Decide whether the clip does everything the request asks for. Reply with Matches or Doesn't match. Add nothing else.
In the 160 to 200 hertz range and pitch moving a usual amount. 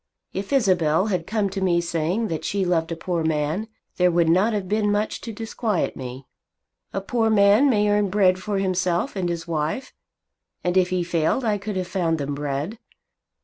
Matches